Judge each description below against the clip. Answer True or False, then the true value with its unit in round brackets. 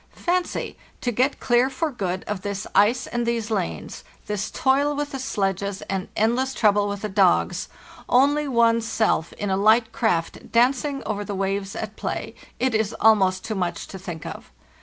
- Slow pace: False (180 wpm)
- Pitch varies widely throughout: False (4.1 semitones)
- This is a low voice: False (215 Hz)